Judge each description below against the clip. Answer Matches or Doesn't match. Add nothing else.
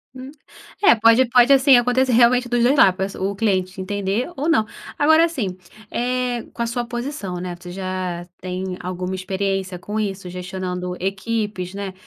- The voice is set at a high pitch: Matches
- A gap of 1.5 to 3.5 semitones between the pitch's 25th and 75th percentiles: Doesn't match